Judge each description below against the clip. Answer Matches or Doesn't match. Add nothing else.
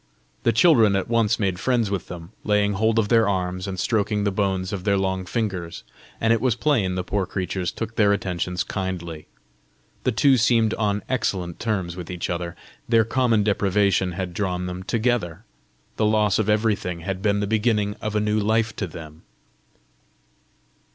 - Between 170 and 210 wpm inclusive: Matches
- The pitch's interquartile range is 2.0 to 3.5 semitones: Matches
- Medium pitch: Doesn't match